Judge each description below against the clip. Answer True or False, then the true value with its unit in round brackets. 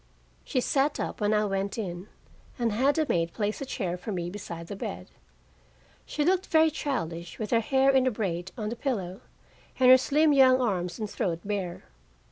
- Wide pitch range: True (6.7 semitones)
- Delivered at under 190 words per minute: False (195 wpm)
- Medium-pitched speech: False (215 Hz)